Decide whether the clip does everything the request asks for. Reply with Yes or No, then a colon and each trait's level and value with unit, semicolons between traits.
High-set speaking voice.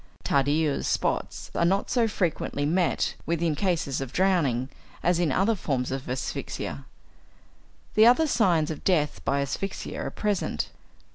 No: medium, 165 Hz